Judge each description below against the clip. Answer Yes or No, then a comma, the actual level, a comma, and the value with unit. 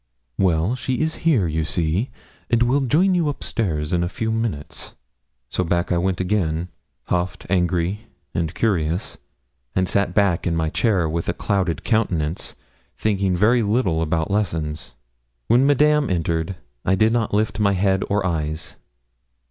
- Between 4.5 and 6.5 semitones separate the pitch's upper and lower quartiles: Yes, average, 5.1 semitones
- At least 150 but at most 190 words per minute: Yes, average, 155 wpm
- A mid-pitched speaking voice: No, very low, 95 Hz